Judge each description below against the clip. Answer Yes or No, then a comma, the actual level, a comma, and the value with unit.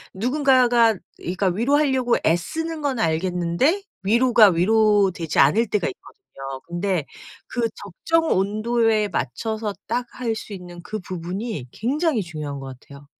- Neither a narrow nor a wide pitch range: No, wide, 5.8 semitones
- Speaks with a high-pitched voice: Yes, high, 215 Hz